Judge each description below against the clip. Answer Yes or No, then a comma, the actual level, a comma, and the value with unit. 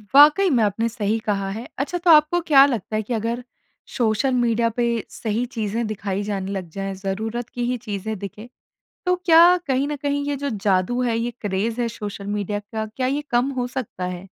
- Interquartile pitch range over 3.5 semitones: Yes, average, 4.2 semitones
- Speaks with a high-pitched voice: Yes, high, 230 Hz